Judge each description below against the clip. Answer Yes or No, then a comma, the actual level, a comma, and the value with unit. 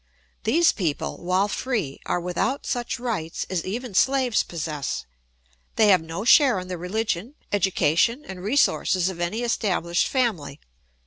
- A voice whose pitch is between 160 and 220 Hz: Yes, high, 190 Hz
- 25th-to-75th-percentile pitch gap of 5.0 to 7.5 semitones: Yes, wide, 5.6 semitones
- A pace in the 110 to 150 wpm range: Yes, average, 140 wpm